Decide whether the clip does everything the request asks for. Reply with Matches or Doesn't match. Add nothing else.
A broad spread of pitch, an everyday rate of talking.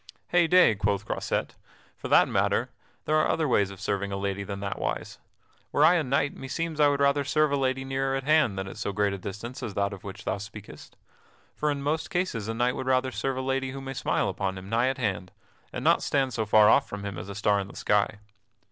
Doesn't match